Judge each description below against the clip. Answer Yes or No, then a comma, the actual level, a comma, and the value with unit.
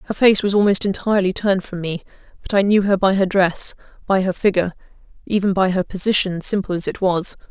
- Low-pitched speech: No, high, 190 Hz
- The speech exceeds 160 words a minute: Yes, average, 200 wpm